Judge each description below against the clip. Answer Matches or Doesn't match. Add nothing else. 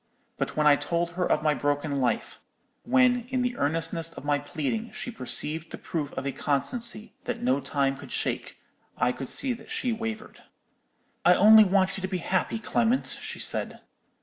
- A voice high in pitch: Doesn't match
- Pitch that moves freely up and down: Matches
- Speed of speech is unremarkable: Matches